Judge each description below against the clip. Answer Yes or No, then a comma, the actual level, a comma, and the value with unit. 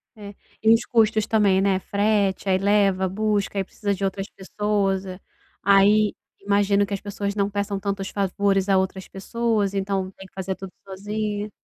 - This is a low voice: No, high, 200 Hz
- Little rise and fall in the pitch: Yes, narrow, 1.2 semitones